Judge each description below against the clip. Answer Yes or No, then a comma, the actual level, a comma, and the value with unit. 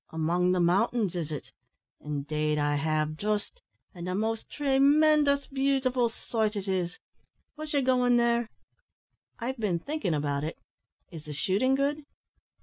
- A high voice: Yes, high, 210 Hz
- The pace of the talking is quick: No, average, 145 wpm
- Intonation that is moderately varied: No, wide, 8.5 semitones